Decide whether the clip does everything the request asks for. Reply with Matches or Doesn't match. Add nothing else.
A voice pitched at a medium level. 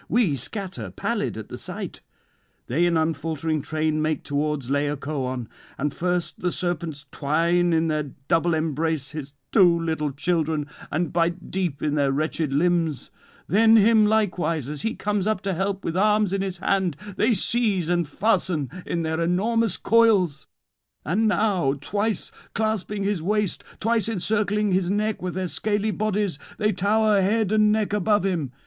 Matches